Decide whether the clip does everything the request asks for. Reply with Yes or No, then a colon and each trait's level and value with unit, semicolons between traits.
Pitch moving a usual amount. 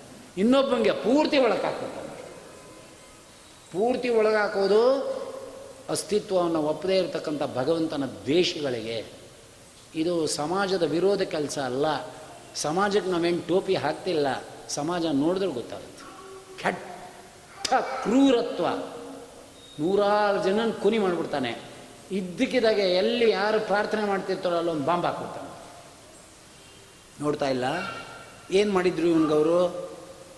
Yes: average, 4.8 semitones